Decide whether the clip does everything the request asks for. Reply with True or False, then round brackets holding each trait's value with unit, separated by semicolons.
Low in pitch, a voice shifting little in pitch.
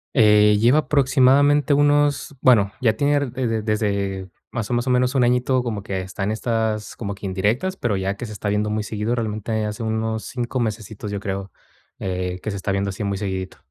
False (110 Hz; 3.7 semitones)